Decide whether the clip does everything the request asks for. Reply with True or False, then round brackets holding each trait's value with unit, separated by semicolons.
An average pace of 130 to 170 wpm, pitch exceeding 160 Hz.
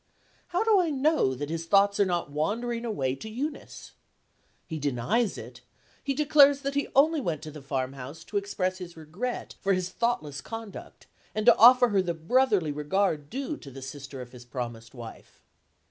False (185 wpm; 185 Hz)